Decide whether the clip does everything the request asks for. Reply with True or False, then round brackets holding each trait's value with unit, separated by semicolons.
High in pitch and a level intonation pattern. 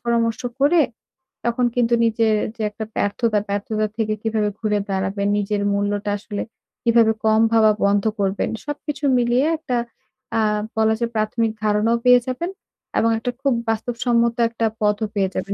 True (225 Hz; 2.2 semitones)